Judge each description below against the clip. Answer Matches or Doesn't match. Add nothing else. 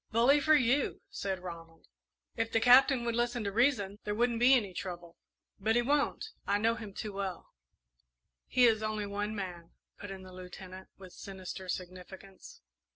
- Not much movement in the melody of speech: Doesn't match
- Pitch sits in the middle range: Doesn't match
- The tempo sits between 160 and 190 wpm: Matches